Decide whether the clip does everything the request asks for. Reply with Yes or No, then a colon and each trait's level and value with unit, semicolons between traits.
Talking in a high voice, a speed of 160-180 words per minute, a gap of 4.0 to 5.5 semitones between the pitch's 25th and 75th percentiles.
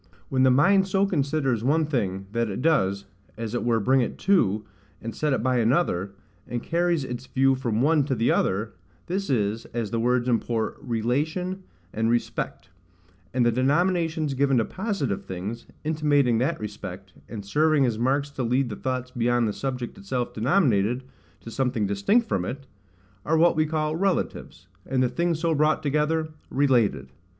No: low, 130 Hz; average, 170 wpm; average, 5.2 semitones